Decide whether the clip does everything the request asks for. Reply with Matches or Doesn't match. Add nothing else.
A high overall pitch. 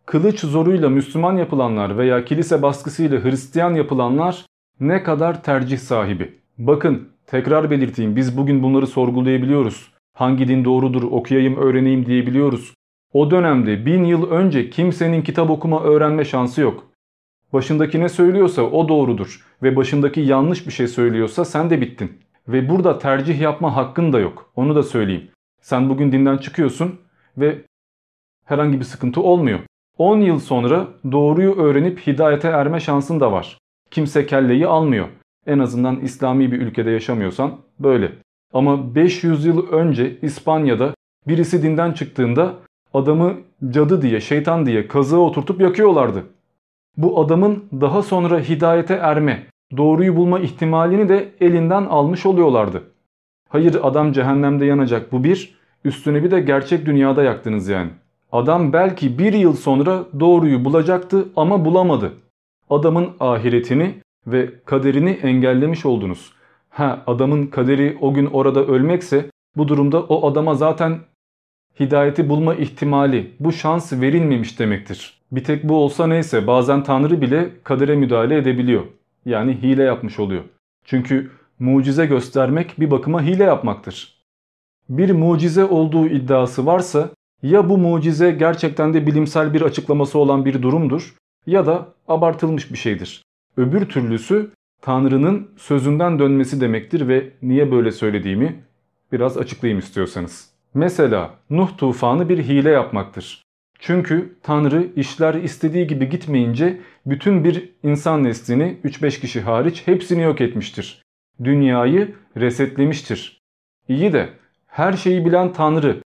Doesn't match